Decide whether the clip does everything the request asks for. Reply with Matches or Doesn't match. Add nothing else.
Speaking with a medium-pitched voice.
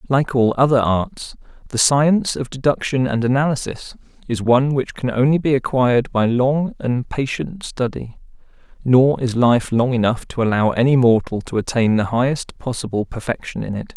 Doesn't match